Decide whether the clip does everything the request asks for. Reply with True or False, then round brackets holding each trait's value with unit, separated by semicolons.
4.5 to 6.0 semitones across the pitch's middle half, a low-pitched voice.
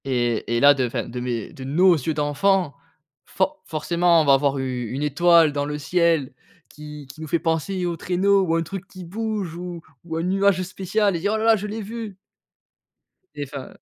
False (5.0 semitones; 165 Hz)